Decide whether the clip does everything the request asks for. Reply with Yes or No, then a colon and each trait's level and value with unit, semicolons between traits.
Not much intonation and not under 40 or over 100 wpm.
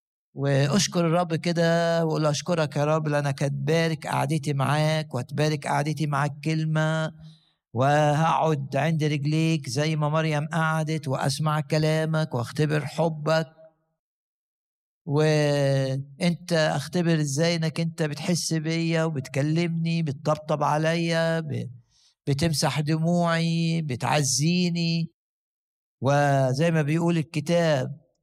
Yes: narrow, 1.9 semitones; average, 90 wpm